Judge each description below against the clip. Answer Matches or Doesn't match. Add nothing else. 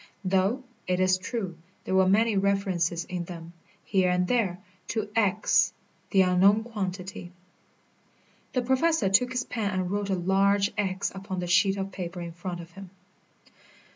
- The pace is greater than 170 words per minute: Doesn't match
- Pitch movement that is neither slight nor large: Doesn't match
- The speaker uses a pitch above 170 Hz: Matches